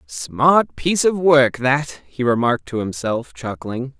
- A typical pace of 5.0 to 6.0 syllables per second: No, 4.0 syllables/s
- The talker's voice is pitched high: No, low, 130 Hz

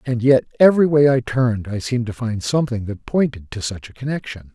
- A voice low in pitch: Yes, low, 120 Hz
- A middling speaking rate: No, fast, 225 wpm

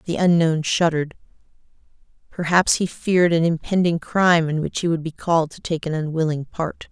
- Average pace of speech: Yes, average, 175 wpm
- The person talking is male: No, female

